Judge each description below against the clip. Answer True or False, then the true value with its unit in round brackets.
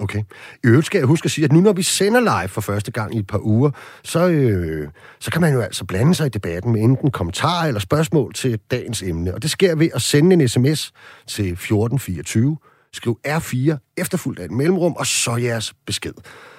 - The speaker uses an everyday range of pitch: False (7.0 semitones)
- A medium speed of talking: True (215 wpm)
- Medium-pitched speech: False (130 Hz)